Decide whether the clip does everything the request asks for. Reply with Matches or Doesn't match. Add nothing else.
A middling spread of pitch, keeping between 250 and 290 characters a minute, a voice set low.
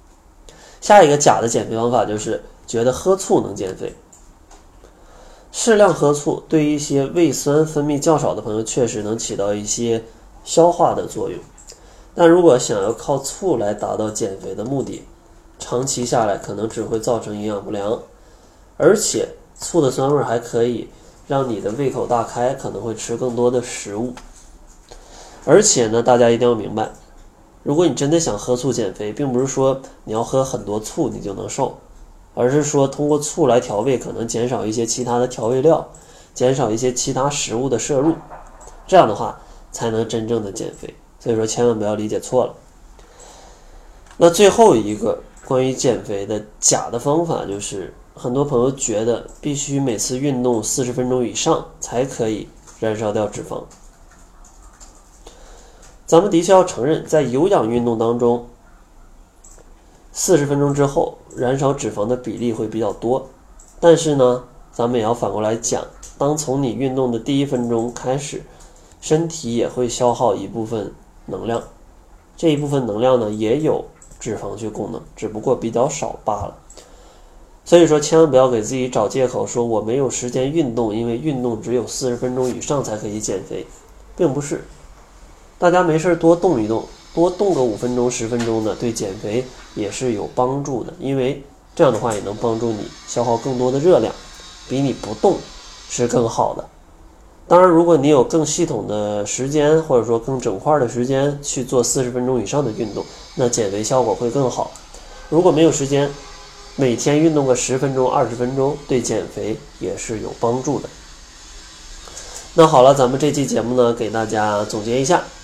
Matches